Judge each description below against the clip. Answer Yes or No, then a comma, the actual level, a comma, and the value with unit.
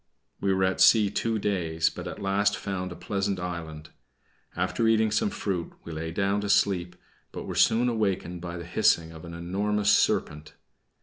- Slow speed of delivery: No, average, 180 wpm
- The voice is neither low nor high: No, very low, 95 Hz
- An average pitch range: Yes, average, 3.2 semitones